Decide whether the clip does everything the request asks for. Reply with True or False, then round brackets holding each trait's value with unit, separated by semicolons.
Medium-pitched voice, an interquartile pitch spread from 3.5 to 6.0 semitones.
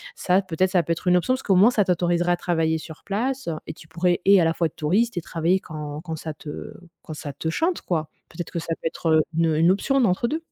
False (175 Hz; 3.1 semitones)